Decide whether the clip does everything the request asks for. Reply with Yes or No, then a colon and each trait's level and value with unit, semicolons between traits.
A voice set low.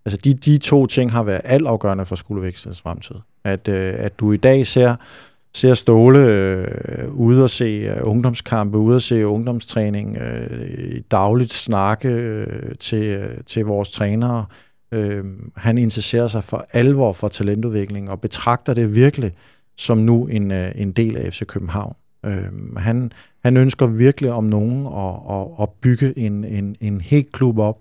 Yes: low, 110 Hz